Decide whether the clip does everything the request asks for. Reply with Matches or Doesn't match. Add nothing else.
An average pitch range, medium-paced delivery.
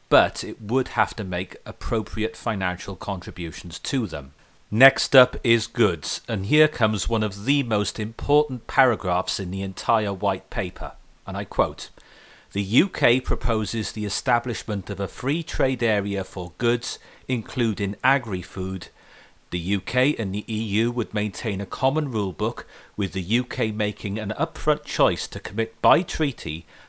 Matches